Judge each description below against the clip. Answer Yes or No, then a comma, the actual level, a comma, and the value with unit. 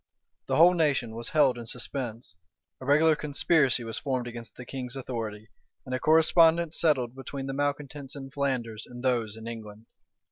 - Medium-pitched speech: No, low, 130 Hz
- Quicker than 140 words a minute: Yes, average, 170 wpm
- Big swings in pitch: No, average, 3.6 semitones